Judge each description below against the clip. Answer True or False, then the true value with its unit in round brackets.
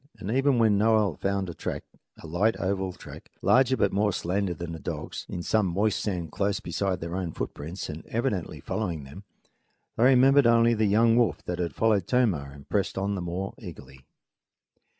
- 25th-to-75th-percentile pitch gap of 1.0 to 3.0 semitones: False (4.3 semitones)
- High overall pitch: False (100 Hz)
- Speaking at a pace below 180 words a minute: False (190 wpm)